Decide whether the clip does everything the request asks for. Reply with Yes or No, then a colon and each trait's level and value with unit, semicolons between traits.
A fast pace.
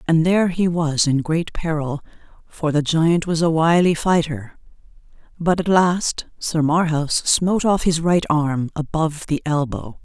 No: average, 160 wpm